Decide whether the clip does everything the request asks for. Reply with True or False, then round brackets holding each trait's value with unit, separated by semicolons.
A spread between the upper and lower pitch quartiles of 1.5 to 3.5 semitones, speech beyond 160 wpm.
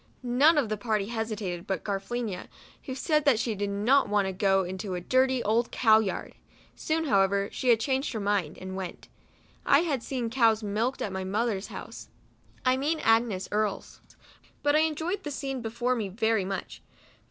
False (4.6 semitones; 185 wpm)